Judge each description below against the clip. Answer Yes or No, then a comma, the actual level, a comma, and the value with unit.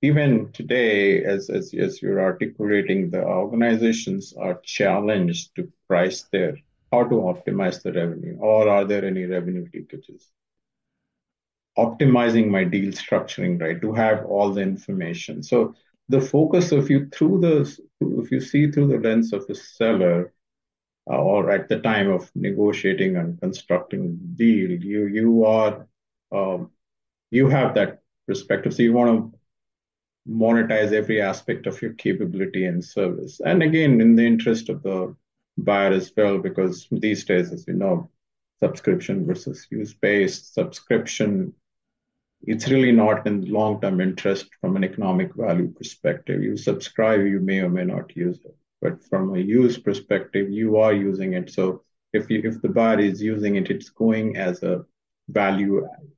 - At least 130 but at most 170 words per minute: Yes, average, 155 wpm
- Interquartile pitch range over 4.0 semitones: Yes, wide, 5.5 semitones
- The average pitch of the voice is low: Yes, low, 110 Hz